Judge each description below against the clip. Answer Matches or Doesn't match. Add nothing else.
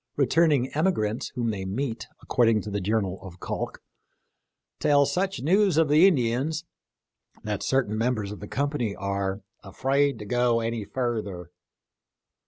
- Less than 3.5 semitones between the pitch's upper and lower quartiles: Doesn't match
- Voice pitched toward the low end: Matches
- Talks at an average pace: Matches